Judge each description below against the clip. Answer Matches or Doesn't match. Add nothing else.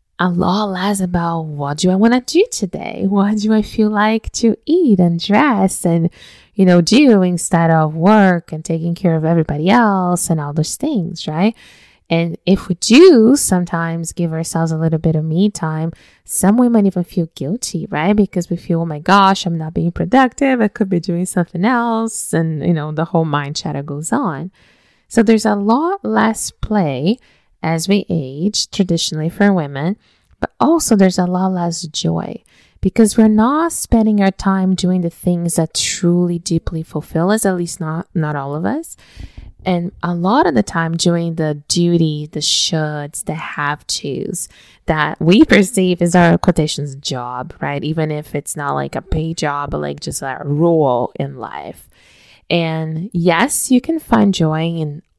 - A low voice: Doesn't match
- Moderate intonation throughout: Matches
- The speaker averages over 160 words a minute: Matches